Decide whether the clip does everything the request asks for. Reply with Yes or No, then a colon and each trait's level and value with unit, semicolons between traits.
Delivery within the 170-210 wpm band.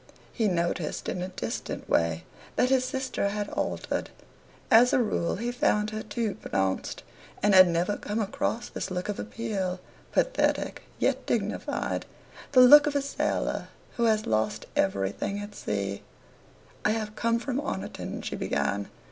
No: average, 155 wpm